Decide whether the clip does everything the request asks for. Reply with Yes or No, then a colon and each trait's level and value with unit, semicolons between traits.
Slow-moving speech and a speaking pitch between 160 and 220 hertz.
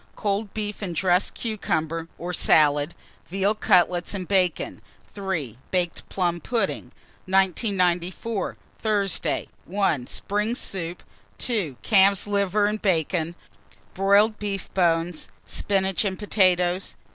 Yes: slow, 110 wpm; high, 190 Hz